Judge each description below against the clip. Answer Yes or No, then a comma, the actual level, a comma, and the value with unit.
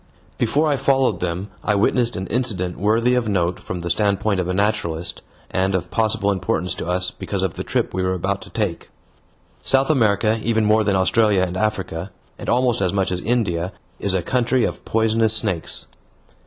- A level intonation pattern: No, average, 3.5 semitones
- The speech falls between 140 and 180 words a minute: No, average, 190 wpm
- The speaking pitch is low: Yes, low, 100 Hz